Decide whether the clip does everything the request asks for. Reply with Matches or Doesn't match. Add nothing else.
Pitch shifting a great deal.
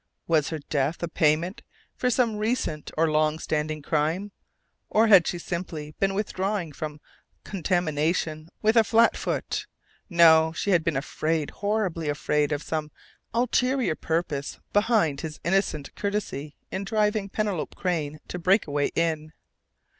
Doesn't match